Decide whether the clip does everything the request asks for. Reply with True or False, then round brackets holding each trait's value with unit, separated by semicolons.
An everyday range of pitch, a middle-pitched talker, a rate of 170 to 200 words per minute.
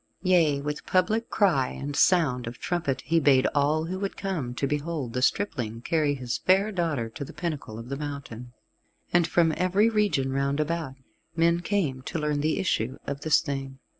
True (4.5 semitones; 150 Hz; 185 wpm)